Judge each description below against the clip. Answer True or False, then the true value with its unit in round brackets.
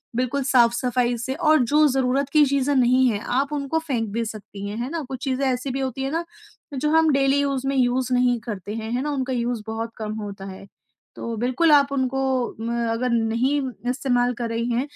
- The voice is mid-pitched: False (255 Hz)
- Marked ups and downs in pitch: False (2.9 semitones)